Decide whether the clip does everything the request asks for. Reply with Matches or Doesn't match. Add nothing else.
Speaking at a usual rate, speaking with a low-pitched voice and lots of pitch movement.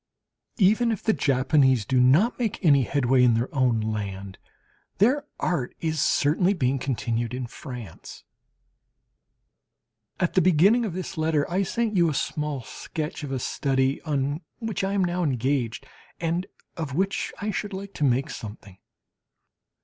Doesn't match